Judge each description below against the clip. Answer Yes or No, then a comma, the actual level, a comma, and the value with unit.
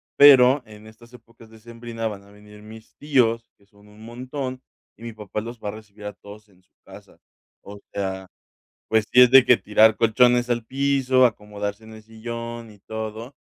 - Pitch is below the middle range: Yes, low, 110 Hz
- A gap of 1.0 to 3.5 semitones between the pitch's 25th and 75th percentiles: Yes, narrow, 2.6 semitones